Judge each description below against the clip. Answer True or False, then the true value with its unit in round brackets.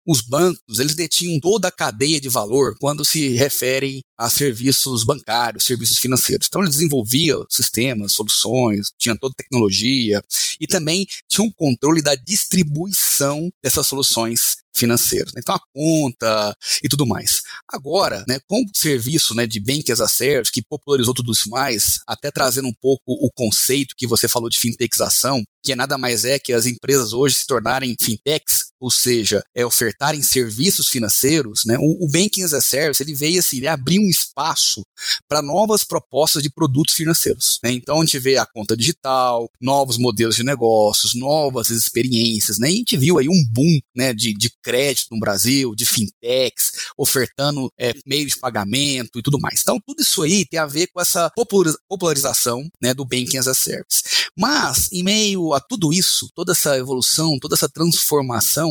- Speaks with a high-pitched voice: False (135 Hz)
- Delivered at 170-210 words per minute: True (175 wpm)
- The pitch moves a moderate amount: True (4.8 semitones)